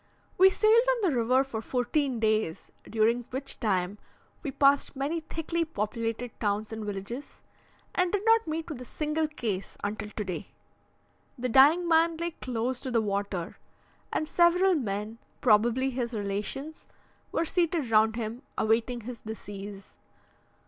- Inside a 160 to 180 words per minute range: No, average, 145 wpm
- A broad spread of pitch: Yes, wide, 6.5 semitones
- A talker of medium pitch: No, high, 245 Hz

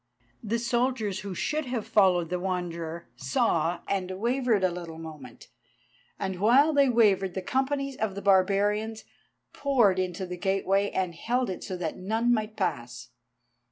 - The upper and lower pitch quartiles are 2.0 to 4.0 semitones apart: No, average, 4.5 semitones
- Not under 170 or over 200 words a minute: No, average, 155 wpm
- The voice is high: Yes, high, 195 Hz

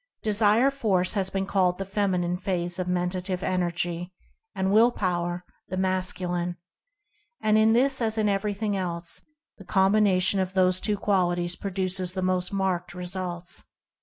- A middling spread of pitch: No, narrow, 2.1 semitones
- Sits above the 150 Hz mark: Yes, medium, 185 Hz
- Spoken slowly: No, average, 155 wpm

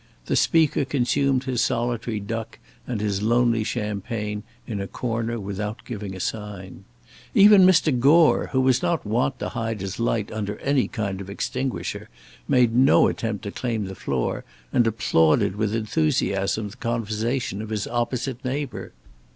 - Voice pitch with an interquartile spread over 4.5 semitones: No, average, 3.5 semitones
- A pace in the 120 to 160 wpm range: Yes, average, 155 wpm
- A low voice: Yes, low, 115 Hz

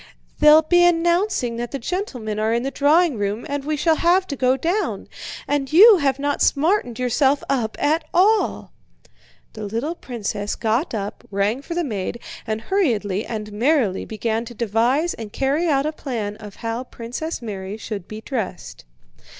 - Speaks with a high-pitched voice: Yes, very high, 255 Hz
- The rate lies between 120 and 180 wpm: Yes, average, 170 wpm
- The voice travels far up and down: Yes, wide, 6.2 semitones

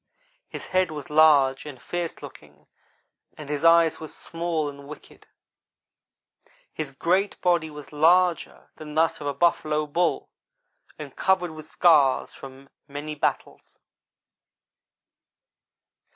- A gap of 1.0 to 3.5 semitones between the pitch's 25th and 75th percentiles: Yes, average, 2.7 semitones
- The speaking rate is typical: No, slow, 120 wpm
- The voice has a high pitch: No, medium, 155 Hz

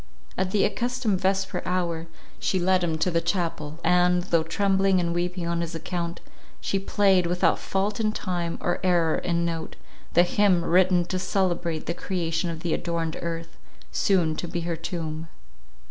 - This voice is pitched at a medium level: Yes, medium, 175 Hz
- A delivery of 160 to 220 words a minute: Yes, average, 170 wpm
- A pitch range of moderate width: No, narrow, 1.9 semitones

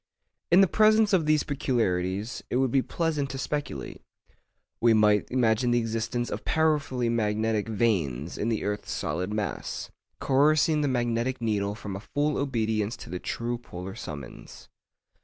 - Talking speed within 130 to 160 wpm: Yes, average, 155 wpm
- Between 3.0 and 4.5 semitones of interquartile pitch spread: No, average, 4.9 semitones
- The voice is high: No, low, 115 Hz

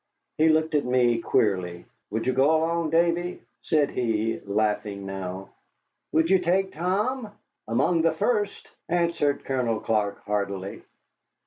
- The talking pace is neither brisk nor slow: No, slow, 130 wpm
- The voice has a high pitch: No, low, 135 Hz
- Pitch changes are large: Yes, wide, 8.2 semitones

